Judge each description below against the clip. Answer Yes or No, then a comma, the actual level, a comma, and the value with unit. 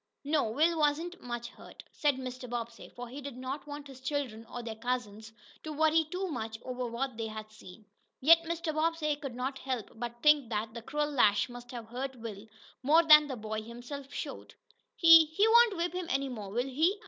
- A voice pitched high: Yes, very high, 260 Hz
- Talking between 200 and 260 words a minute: Yes, fast, 205 wpm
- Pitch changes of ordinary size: Yes, average, 4.6 semitones